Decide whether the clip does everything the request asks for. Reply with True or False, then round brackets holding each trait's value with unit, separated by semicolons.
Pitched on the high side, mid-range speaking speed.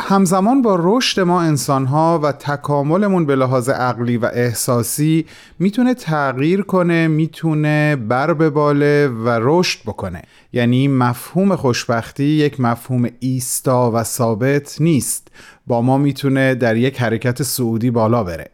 False (140 Hz; 135 wpm)